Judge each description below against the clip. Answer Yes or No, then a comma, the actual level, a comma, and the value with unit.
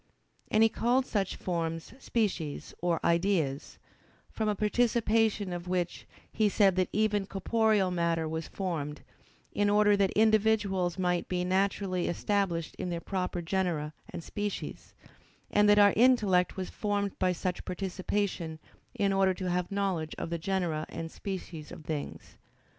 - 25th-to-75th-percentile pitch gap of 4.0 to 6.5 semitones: No, average, 3.2 semitones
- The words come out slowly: No, average, 145 wpm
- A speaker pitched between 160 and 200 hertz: Yes, high, 190 Hz